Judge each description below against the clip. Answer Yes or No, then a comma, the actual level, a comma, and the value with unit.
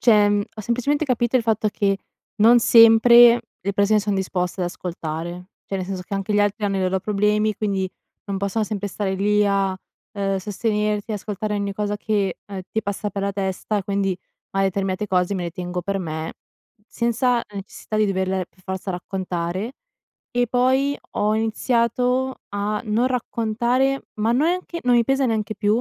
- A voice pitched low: No, high, 205 Hz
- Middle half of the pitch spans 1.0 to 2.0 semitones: No, average, 2.9 semitones